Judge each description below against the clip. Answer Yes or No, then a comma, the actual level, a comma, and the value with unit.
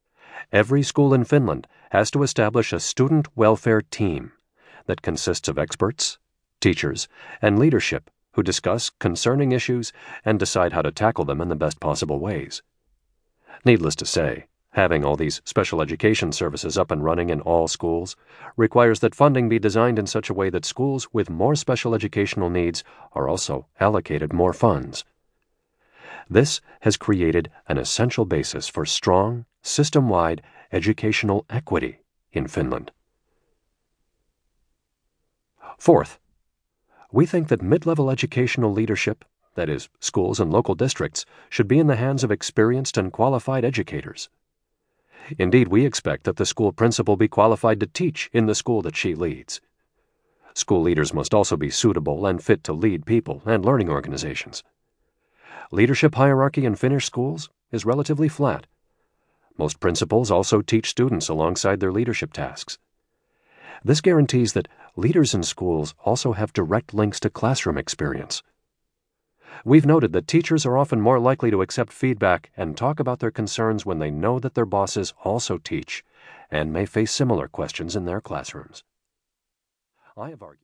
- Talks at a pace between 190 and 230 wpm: No, average, 150 wpm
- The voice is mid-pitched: No, low, 115 Hz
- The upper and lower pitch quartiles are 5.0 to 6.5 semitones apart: No, average, 4.4 semitones